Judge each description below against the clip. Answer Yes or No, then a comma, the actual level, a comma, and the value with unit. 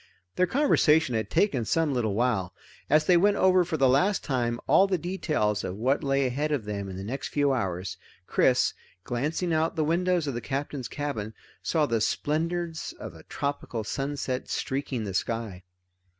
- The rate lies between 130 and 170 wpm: No, average, 180 wpm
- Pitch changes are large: Yes, wide, 5.9 semitones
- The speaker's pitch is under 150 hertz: Yes, medium, 140 Hz